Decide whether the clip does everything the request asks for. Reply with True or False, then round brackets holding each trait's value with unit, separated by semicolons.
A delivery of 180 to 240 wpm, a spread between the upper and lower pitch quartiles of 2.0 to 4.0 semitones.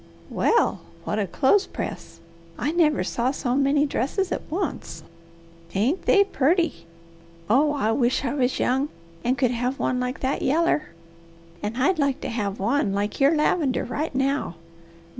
False (155 wpm; 3.6 semitones)